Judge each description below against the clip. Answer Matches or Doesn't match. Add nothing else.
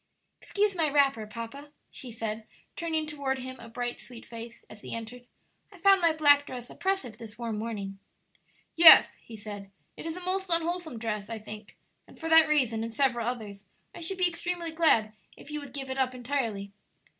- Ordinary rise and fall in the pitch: Doesn't match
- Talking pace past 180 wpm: Matches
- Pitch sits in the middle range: Doesn't match